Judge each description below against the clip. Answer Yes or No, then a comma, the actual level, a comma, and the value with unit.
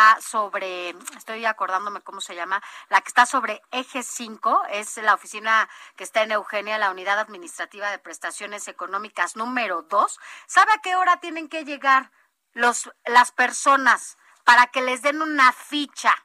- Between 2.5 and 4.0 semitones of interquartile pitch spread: No, average, 4.8 semitones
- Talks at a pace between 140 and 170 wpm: Yes, average, 160 wpm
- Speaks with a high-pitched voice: Yes, high, 225 Hz